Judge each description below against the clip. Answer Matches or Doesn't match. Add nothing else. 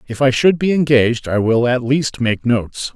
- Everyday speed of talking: Doesn't match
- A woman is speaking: Doesn't match